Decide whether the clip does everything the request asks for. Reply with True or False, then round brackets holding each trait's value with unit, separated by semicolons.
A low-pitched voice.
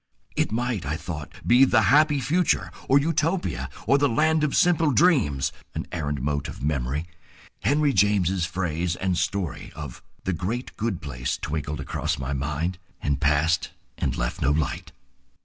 True (90 Hz)